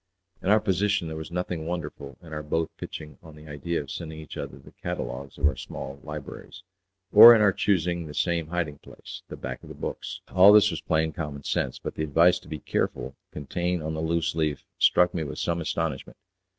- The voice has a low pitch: Yes, very low, 80 Hz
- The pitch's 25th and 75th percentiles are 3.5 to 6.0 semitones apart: No, average, 2.7 semitones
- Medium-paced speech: No, fast, 215 wpm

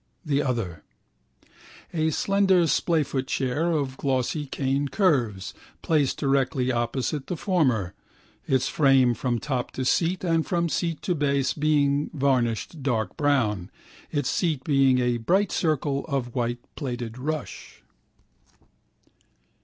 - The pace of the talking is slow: Yes, slow, 120 wpm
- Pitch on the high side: No, medium, 140 Hz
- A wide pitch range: No, average, 3.7 semitones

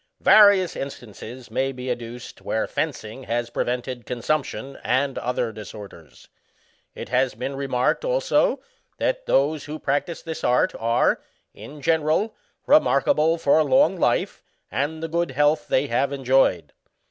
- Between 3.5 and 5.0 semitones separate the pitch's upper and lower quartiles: Yes, average, 4.3 semitones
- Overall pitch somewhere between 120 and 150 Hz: Yes, low, 135 Hz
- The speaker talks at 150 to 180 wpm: No, average, 140 wpm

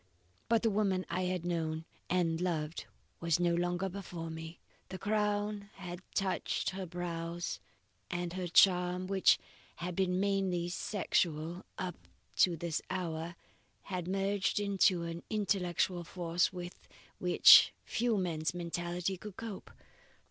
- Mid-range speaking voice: Yes, medium, 180 Hz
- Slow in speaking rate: Yes, slow, 130 wpm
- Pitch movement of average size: No, narrow, 2.1 semitones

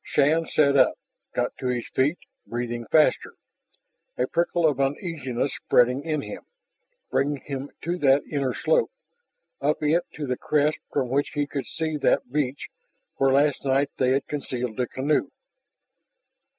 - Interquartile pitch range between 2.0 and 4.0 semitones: Yes, narrow, 2.5 semitones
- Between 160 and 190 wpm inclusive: No, average, 150 wpm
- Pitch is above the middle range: No, medium, 140 Hz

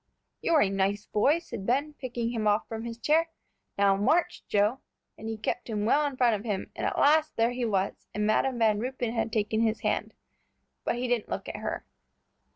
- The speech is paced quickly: Yes, fast, 210 wpm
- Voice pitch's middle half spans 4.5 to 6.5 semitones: No, average, 3.4 semitones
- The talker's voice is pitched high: Yes, high, 230 Hz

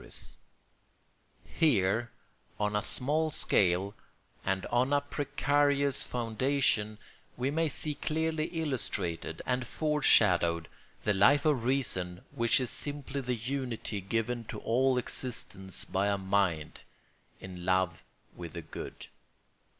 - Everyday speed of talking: No, slow, 120 wpm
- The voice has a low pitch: Yes, low, 120 Hz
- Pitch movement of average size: No, wide, 6.8 semitones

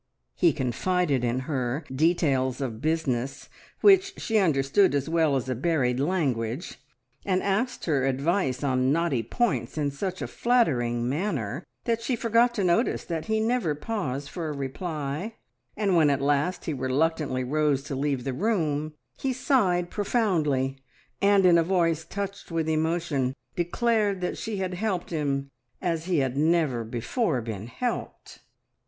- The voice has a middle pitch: Yes, medium, 160 Hz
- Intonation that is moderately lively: No, wide, 5.9 semitones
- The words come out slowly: No, average, 155 wpm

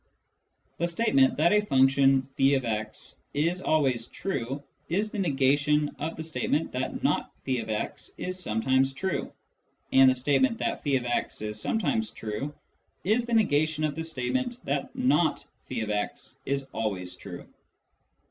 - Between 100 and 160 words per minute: Yes, average, 140 wpm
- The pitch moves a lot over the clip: No, average, 4.9 semitones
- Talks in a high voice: No, medium, 140 Hz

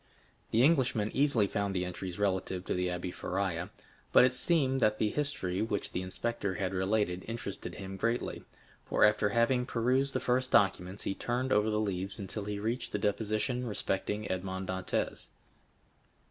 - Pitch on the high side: No, low, 105 Hz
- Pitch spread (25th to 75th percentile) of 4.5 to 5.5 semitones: No, average, 3.9 semitones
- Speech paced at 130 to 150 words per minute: No, average, 165 wpm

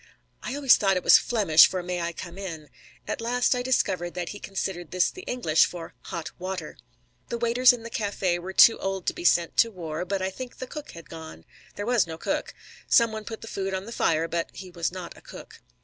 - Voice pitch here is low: No, high, 190 Hz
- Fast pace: Yes, fast, 235 wpm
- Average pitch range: Yes, average, 4.9 semitones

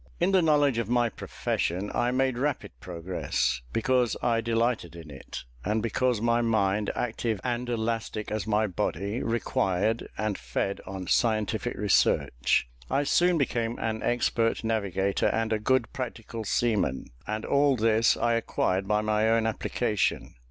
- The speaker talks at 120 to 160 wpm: Yes, average, 150 wpm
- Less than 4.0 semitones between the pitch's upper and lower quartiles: Yes, narrow, 2.6 semitones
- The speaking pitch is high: No, low, 115 Hz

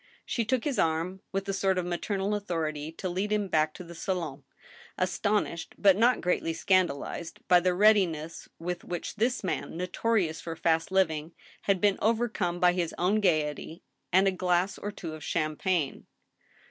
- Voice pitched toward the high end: No, medium, 180 Hz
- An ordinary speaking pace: Yes, average, 170 wpm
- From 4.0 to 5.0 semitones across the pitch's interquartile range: No, average, 3.2 semitones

